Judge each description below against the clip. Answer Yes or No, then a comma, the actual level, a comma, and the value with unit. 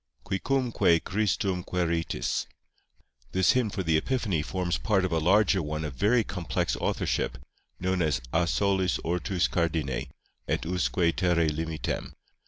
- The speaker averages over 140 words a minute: No, slow, 135 wpm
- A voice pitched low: Yes, very low, 90 Hz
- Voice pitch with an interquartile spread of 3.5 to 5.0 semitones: No, average, 3.0 semitones